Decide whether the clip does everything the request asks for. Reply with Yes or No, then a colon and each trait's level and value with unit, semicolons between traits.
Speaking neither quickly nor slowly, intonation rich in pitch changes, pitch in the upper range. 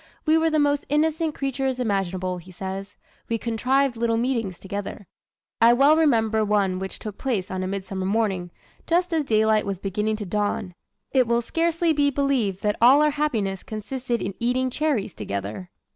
Yes: average, 175 wpm; wide, 5.9 semitones; high, 225 Hz